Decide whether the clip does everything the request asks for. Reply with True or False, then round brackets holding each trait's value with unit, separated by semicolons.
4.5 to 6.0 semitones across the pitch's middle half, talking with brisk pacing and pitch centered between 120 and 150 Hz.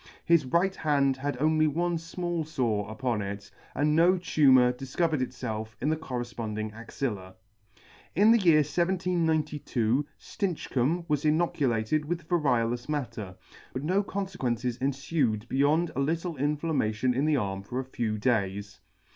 False (5.4 semitones; 140 wpm; 140 Hz)